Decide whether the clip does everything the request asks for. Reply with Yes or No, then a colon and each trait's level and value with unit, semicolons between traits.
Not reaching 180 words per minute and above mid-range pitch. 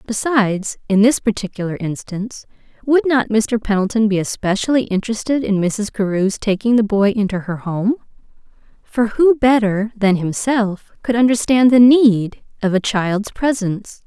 Yes: average, 140 wpm; high, 215 Hz